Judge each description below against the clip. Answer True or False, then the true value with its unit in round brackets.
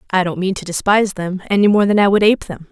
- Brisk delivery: True (285 wpm)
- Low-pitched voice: False (195 Hz)